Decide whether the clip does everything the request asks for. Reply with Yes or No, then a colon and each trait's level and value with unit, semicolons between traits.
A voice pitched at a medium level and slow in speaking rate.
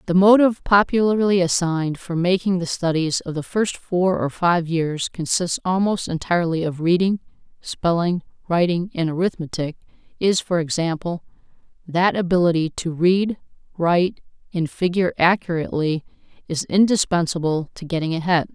Yes: medium, 175 Hz; slow, 130 wpm